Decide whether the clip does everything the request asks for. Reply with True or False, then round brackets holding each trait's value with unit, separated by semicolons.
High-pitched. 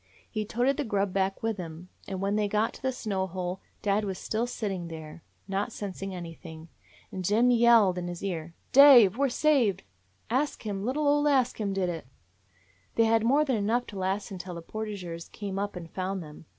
True (200 Hz)